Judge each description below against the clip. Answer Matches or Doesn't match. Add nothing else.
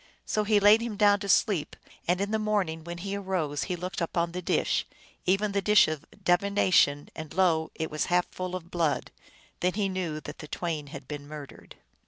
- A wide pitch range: Doesn't match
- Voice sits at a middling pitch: Matches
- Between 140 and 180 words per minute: Doesn't match